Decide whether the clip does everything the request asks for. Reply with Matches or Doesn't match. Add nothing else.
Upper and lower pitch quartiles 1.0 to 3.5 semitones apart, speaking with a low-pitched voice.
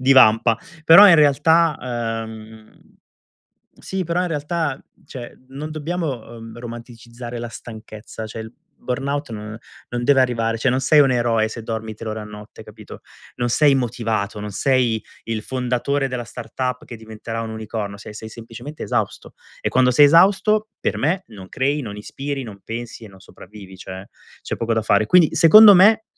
Doesn't match